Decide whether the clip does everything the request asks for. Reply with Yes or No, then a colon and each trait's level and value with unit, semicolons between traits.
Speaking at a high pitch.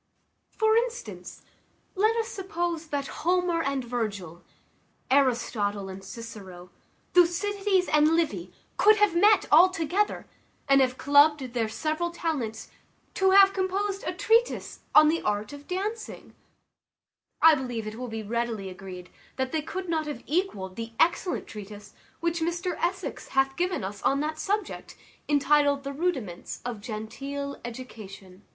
Yes: very high, 290 Hz